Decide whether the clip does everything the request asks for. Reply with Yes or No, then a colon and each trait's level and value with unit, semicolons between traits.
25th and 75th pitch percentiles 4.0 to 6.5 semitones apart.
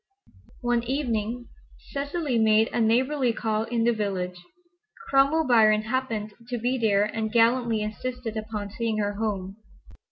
No: narrow, 2.6 semitones